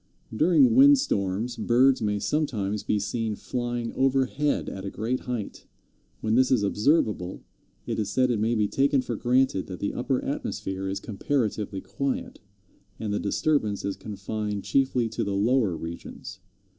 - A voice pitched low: Yes, low, 115 Hz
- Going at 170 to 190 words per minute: No, average, 155 wpm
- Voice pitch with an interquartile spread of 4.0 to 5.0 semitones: Yes, average, 4.5 semitones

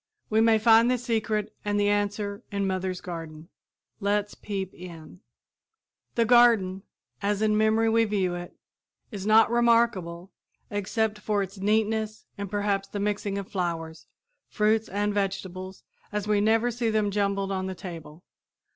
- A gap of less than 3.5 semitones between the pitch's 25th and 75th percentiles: Yes, narrow, 2.4 semitones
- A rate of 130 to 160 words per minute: Yes, average, 150 wpm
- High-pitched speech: Yes, high, 205 Hz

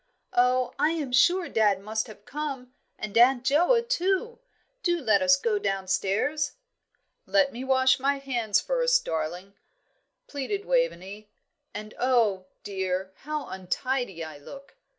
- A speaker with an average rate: No, slow, 130 wpm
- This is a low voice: No, very high, 255 Hz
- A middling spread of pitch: No, wide, 6.7 semitones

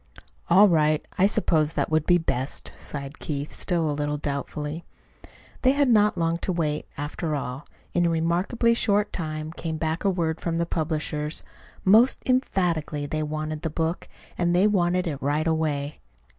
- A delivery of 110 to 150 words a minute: No, average, 165 wpm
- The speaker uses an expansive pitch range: No, average, 2.8 semitones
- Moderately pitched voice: Yes, medium, 160 Hz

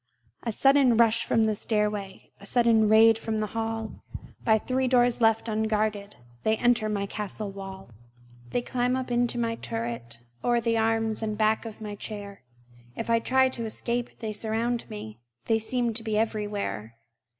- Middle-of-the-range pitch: No, high, 220 Hz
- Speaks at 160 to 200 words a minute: Yes, average, 170 wpm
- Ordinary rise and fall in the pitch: No, narrow, 1.9 semitones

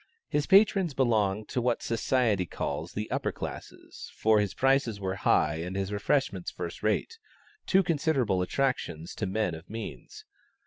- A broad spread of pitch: Yes, wide, 6.1 semitones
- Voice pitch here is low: Yes, low, 110 Hz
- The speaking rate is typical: Yes, average, 150 wpm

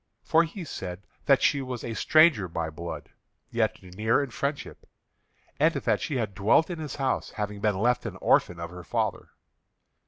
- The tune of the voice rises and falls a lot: Yes, wide, 7.2 semitones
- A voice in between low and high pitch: No, low, 115 Hz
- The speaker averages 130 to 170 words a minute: No, average, 180 wpm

